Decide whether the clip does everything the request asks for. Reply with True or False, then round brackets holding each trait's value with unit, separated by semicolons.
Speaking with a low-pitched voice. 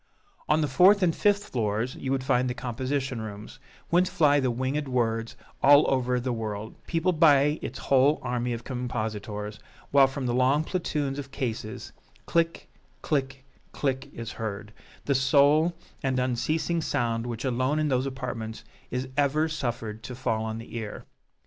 True (130 Hz)